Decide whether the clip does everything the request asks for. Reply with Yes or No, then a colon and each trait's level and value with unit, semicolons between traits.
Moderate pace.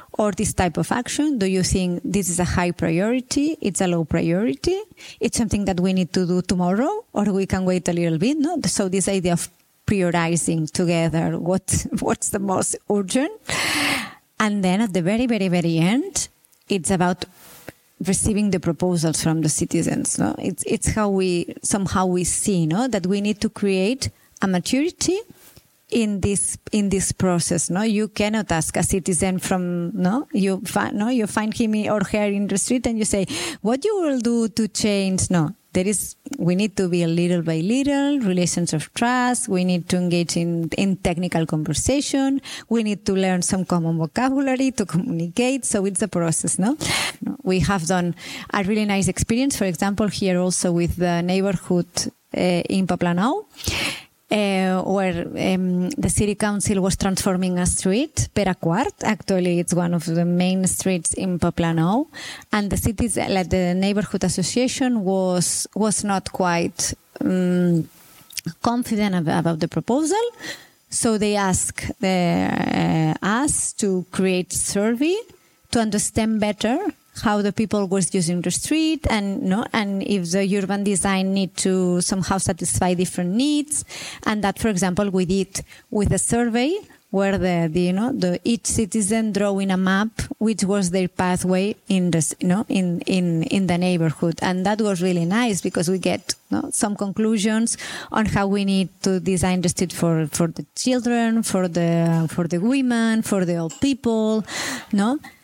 No: fast, 170 wpm